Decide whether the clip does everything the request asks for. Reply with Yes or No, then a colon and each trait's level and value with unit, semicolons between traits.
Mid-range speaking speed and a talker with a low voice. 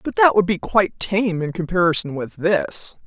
No: average, 195 wpm; medium, 180 Hz